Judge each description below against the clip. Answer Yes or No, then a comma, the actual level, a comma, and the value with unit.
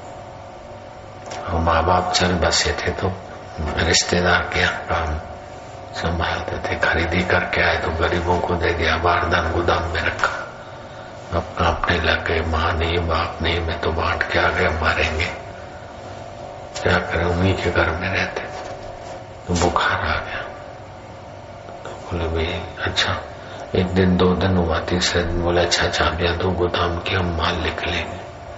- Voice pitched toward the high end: No, very low, 85 Hz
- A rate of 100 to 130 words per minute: No, average, 150 wpm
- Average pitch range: No, narrow, 1.4 semitones